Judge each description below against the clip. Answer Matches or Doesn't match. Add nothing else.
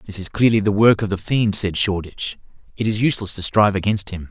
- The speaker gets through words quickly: Matches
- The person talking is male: Matches